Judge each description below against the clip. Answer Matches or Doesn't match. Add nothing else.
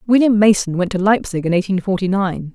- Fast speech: Matches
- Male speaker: Doesn't match